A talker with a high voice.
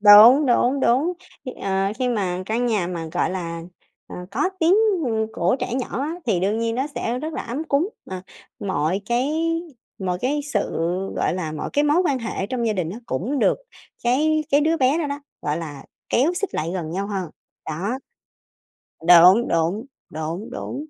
Yes: high, 225 Hz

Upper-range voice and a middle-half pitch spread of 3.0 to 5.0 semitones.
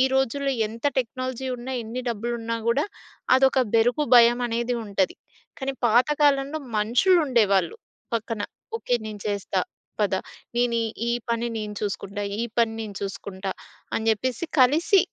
Yes: high, 235 Hz; average, 3.4 semitones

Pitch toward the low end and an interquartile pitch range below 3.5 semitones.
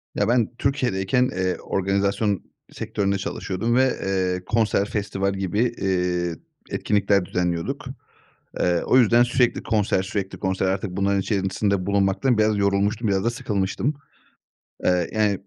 Yes: low, 100 Hz; narrow, 2.5 semitones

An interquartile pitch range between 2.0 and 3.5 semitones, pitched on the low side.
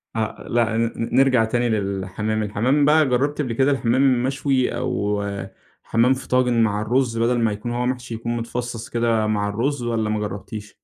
Yes: average, 2.8 semitones; low, 115 Hz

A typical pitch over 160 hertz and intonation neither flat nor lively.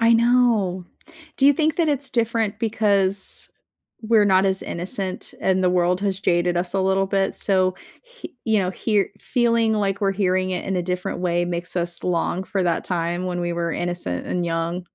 Yes: high, 190 Hz; average, 3.3 semitones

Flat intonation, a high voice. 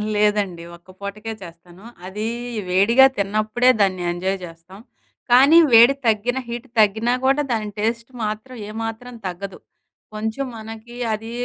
No: average, 3.3 semitones; high, 215 Hz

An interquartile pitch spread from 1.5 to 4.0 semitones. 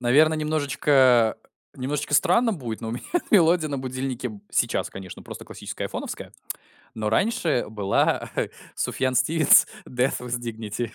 No: average, 4.8 semitones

